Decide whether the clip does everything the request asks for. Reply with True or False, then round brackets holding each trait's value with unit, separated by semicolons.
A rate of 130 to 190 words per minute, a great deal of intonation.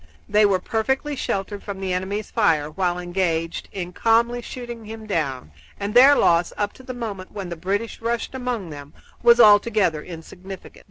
False (170 wpm; 4.6 semitones)